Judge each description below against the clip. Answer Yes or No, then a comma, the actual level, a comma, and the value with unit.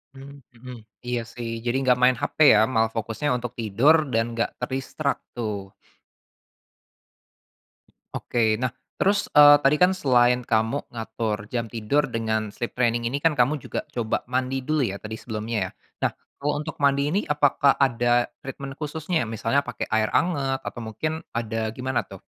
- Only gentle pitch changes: No, average, 3.7 semitones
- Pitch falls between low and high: No, low, 125 Hz